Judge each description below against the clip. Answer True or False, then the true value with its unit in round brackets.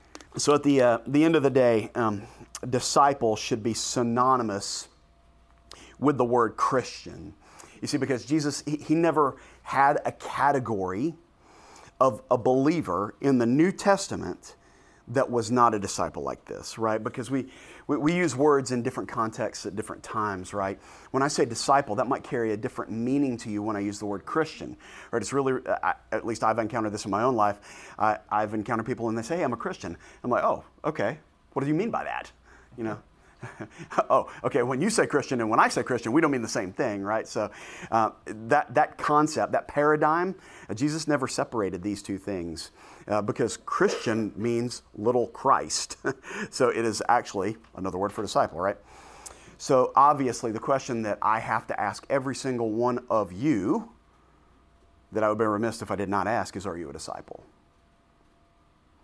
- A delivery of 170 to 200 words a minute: True (185 wpm)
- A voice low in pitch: True (115 Hz)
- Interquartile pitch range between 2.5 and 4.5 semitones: False (5.1 semitones)